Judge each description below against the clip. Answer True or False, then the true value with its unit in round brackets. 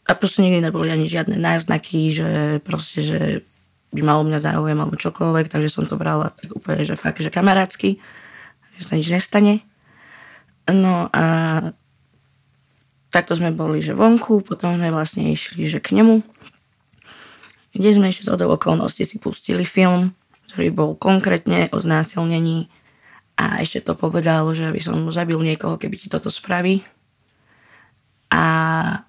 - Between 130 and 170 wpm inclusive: True (150 wpm)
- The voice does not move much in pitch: False (3.7 semitones)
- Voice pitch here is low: False (165 Hz)